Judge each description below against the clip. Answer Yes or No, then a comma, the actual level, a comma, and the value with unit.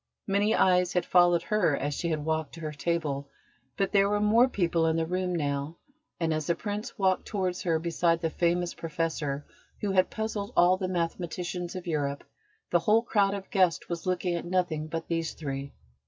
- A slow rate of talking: No, average, 195 wpm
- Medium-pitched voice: Yes, medium, 175 Hz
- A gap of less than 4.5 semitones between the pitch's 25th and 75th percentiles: Yes, average, 2.7 semitones